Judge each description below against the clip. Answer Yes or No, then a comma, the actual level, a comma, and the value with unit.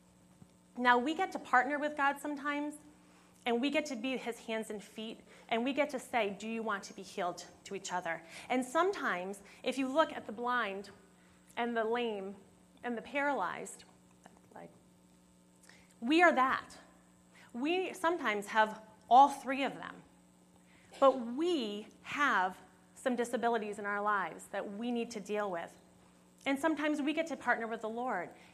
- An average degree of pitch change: No, wide, 5.7 semitones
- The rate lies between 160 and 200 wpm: Yes, average, 165 wpm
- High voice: Yes, high, 230 Hz